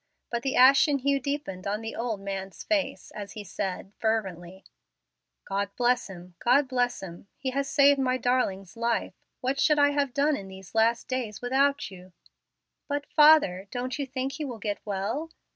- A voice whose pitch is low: No, high, 245 Hz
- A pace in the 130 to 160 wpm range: No, average, 175 wpm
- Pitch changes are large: Yes, wide, 5.7 semitones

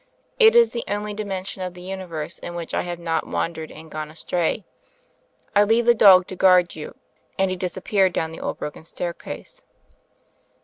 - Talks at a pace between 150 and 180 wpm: No, average, 190 wpm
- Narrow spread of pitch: No, average, 3.3 semitones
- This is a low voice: No, medium, 185 Hz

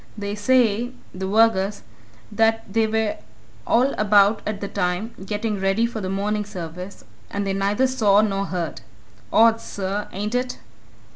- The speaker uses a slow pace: No, average, 150 wpm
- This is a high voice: Yes, high, 210 Hz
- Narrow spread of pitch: Yes, narrow, 2.3 semitones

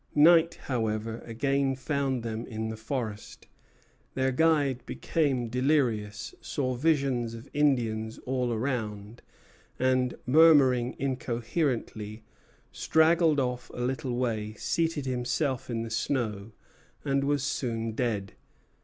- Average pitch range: Yes, average, 3.6 semitones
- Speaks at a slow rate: Yes, slow, 110 wpm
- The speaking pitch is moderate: No, low, 125 Hz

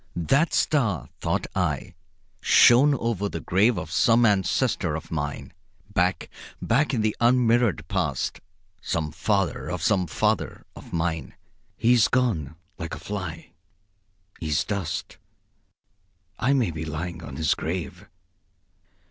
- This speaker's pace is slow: Yes, slow, 130 wpm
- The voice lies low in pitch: Yes, very low, 95 Hz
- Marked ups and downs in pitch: Yes, wide, 6.4 semitones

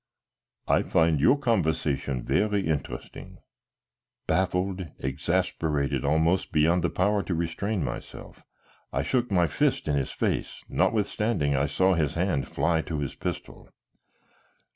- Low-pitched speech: Yes, very low, 85 Hz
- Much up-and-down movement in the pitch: No, average, 4.6 semitones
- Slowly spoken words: Yes, slow, 125 wpm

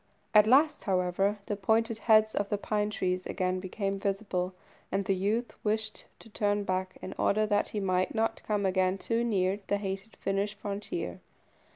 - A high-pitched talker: Yes, high, 205 Hz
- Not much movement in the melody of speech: Yes, narrow, 2.2 semitones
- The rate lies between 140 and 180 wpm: Yes, average, 175 wpm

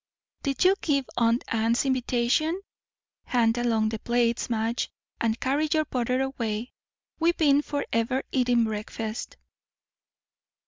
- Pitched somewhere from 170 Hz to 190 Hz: No, high, 240 Hz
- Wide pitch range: No, average, 3.2 semitones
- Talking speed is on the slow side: Yes, slow, 125 wpm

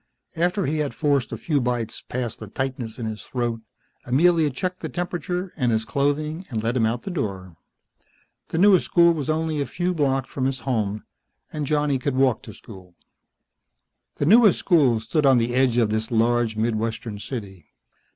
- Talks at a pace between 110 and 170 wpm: No, average, 180 wpm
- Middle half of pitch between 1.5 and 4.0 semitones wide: No, wide, 5.4 semitones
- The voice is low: Yes, low, 130 Hz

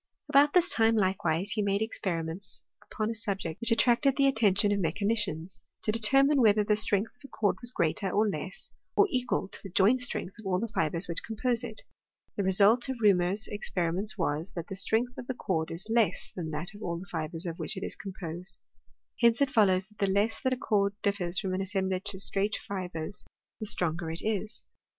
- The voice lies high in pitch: Yes, high, 200 Hz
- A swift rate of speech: Yes, fast, 210 wpm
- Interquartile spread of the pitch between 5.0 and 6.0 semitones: No, average, 3.7 semitones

